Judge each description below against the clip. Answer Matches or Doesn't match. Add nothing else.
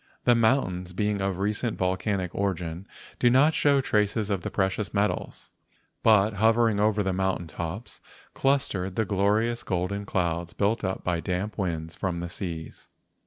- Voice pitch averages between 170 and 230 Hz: Doesn't match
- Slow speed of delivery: Doesn't match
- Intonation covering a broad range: Doesn't match